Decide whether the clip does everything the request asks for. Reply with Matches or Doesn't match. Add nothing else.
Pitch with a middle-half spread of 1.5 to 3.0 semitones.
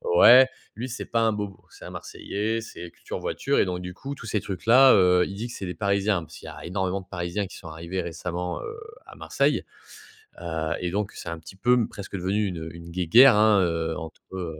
Doesn't match